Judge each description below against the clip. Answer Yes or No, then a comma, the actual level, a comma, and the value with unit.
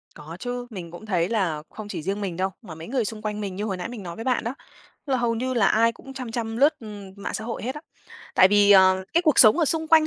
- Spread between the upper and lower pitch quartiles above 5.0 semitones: No, average, 4.4 semitones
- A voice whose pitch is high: Yes, high, 215 Hz